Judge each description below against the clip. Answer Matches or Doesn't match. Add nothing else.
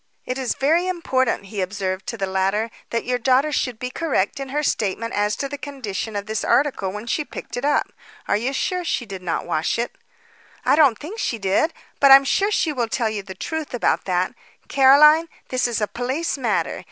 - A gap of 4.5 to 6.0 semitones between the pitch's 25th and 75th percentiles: Matches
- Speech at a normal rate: Doesn't match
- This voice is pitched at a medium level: Doesn't match